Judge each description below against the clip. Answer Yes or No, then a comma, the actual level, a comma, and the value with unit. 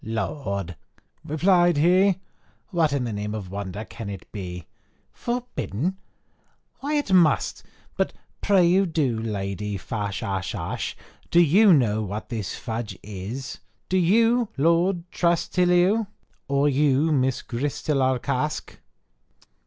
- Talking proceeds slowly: Yes, slow, 115 wpm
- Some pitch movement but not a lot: No, wide, 8.9 semitones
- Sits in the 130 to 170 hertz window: Yes, medium, 140 Hz